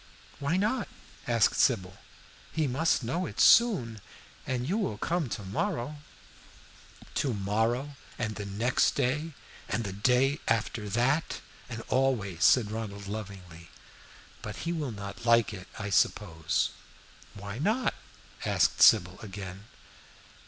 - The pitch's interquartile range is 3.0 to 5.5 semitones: Yes, average, 5.2 semitones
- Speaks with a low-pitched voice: Yes, low, 115 Hz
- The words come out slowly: Yes, slow, 130 wpm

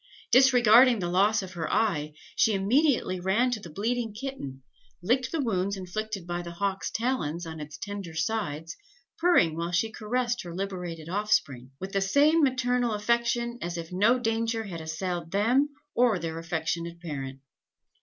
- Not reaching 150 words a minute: No, average, 160 wpm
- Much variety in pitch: Yes, wide, 5.8 semitones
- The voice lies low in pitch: No, high, 195 Hz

